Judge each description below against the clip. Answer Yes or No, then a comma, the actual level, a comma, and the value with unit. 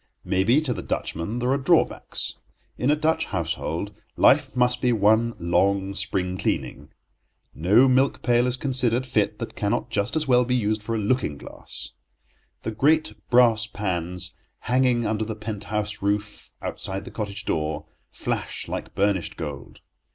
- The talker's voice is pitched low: Yes, low, 110 Hz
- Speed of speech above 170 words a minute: No, average, 160 wpm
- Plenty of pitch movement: No, average, 4.2 semitones